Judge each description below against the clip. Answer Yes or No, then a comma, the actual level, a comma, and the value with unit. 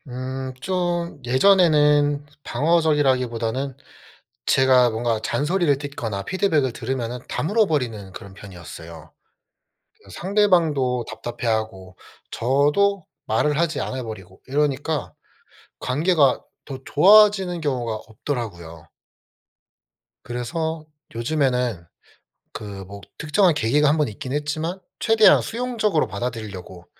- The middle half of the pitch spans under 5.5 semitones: No, wide, 5.8 semitones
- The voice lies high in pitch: No, low, 135 Hz